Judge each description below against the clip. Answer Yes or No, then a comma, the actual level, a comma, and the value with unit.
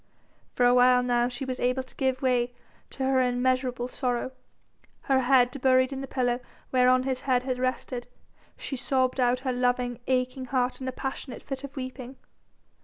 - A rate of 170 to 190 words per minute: Yes, average, 180 wpm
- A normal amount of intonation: No, narrow, 1.0 semitones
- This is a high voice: Yes, very high, 255 Hz